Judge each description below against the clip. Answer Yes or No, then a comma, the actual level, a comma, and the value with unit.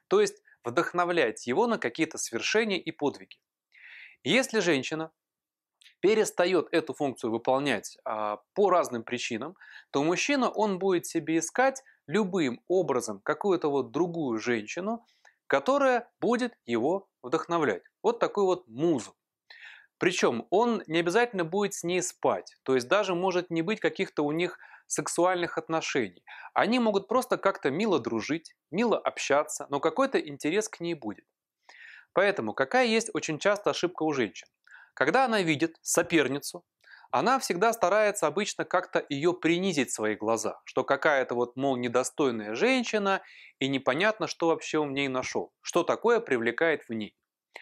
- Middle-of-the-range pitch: Yes, medium, 170 Hz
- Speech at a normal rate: Yes, average, 140 wpm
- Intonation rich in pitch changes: Yes, wide, 6.8 semitones